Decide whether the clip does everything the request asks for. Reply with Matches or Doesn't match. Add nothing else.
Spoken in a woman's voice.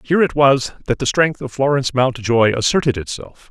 Doesn't match